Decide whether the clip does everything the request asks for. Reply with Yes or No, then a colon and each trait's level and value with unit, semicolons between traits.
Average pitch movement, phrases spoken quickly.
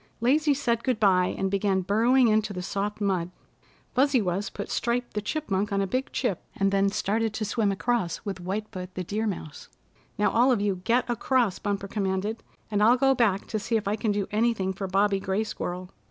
Yes: average, 3.3 semitones; fast, 210 wpm